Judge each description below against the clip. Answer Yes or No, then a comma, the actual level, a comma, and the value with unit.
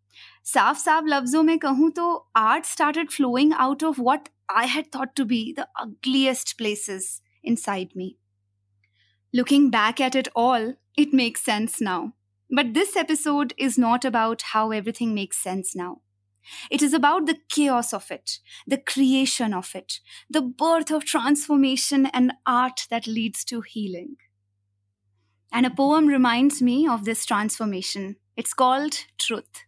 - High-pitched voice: Yes, very high, 250 Hz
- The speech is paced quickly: No, average, 145 wpm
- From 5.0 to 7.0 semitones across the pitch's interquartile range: Yes, average, 5.3 semitones